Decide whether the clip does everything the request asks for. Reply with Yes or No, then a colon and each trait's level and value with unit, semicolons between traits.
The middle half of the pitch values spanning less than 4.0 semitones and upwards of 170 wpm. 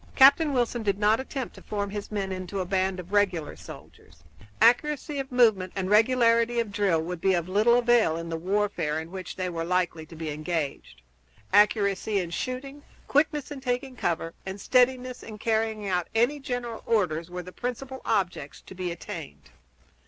No: average, 5.3 semitones; average, 180 wpm